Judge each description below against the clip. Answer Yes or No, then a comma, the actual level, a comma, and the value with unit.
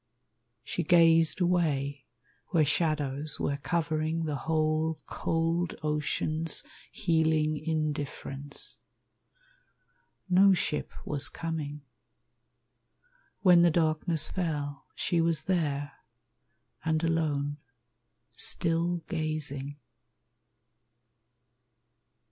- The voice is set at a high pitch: No, medium, 155 Hz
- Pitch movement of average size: No, narrow, 2.1 semitones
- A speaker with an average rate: No, slow, 75 wpm